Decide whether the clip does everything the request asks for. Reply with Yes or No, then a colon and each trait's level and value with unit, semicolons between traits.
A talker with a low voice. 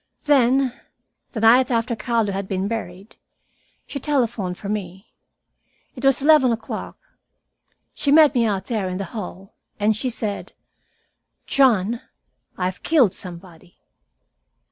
No: high, 225 Hz